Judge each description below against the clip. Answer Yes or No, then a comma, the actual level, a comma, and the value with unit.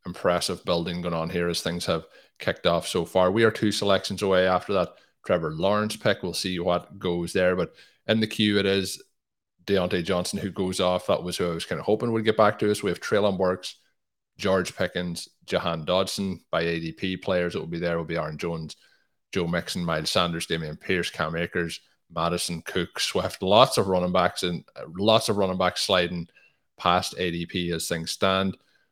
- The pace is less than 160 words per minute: No, average, 200 wpm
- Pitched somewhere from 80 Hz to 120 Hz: Yes, very low, 90 Hz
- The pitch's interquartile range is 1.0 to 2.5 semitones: Yes, narrow, 2.2 semitones